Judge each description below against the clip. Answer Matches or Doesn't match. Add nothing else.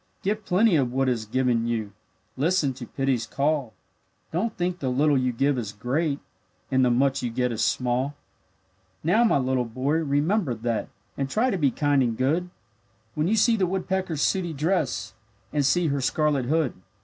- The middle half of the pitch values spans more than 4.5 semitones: Matches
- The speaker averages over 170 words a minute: Matches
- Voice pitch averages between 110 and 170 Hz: Matches